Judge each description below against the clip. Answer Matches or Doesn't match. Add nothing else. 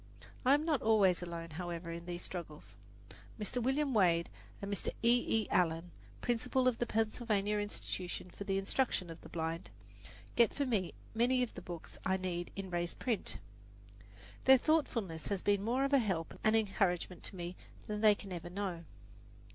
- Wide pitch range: Doesn't match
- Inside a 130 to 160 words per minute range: Doesn't match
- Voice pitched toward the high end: Matches